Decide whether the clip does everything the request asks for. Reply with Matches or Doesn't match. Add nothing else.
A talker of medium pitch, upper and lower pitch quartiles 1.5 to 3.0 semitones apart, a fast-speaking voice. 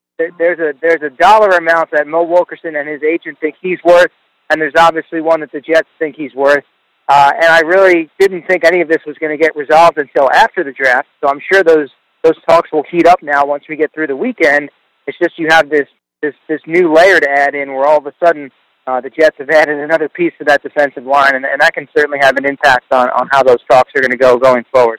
Matches